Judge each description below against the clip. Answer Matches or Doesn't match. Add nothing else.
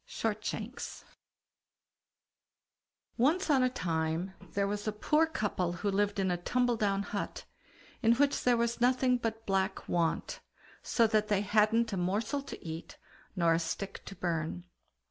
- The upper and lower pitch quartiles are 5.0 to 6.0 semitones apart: Doesn't match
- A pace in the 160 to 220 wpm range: Doesn't match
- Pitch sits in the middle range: Doesn't match